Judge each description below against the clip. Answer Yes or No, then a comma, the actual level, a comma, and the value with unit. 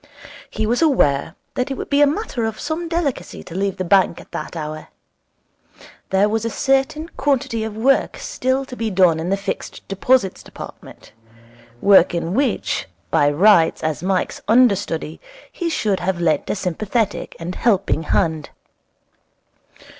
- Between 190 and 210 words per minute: No, average, 155 wpm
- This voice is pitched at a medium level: No, high, 205 Hz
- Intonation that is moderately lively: No, wide, 6.8 semitones